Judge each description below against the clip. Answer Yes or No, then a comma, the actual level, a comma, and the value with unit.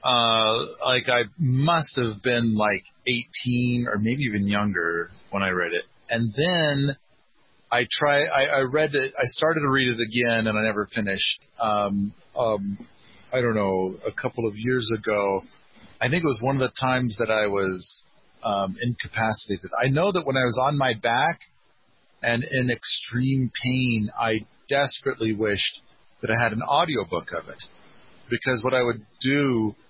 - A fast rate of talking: No, average, 170 wpm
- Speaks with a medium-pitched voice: No, low, 120 Hz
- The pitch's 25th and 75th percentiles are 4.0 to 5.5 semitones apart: No, average, 3.3 semitones